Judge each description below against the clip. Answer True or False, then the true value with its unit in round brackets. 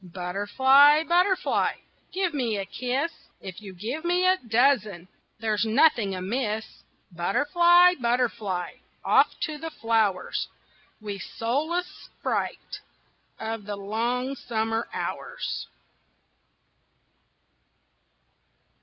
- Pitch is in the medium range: False (235 Hz)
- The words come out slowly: True (90 wpm)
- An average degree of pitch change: False (6.5 semitones)